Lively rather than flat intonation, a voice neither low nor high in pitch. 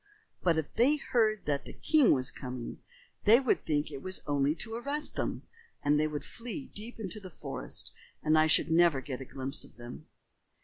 Yes: wide, 7.9 semitones; medium, 160 Hz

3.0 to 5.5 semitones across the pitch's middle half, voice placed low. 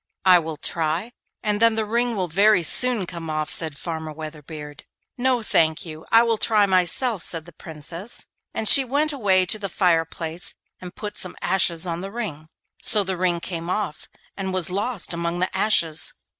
No: average, 4.6 semitones; medium, 180 Hz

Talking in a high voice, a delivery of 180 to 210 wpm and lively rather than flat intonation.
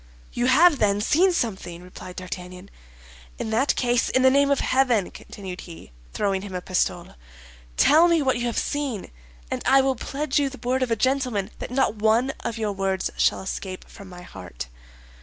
Yes: high, 230 Hz; average, 190 wpm; wide, 5.9 semitones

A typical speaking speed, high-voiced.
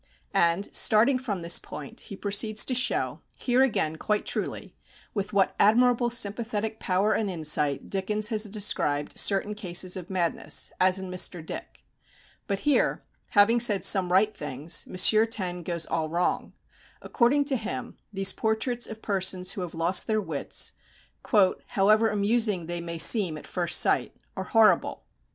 Yes: average, 155 wpm; high, 200 Hz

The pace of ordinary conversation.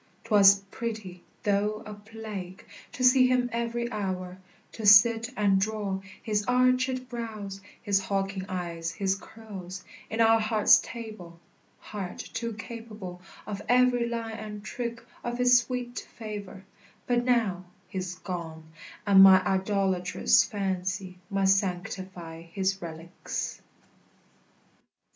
No: slow, 120 wpm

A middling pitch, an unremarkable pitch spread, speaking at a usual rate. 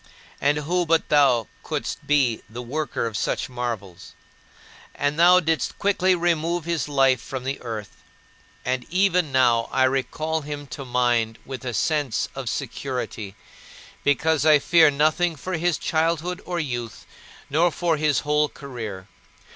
Yes: medium, 145 Hz; average, 4.7 semitones; average, 145 wpm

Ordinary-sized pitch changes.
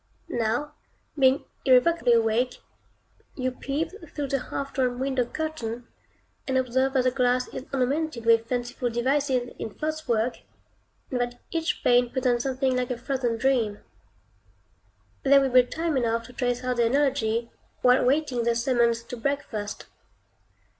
No: narrow, 2.3 semitones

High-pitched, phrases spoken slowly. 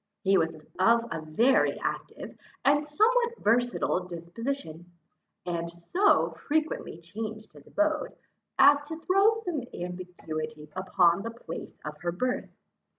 Yes: high, 210 Hz; slow, 125 wpm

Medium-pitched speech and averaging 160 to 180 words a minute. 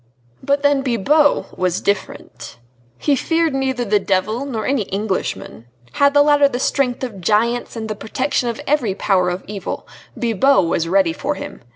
No: high, 235 Hz; average, 170 wpm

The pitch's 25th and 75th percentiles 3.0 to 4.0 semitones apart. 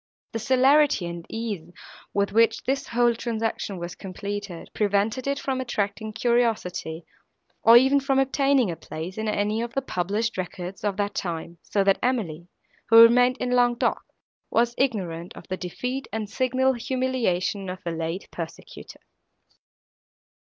No: average, 5.2 semitones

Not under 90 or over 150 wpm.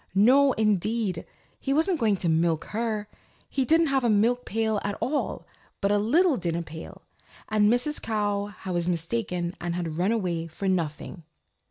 No: average, 165 wpm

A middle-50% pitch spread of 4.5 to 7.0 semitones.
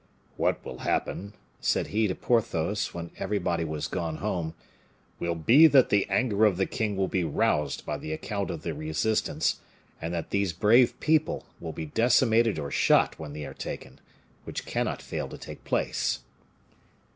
Yes: wide, 5.4 semitones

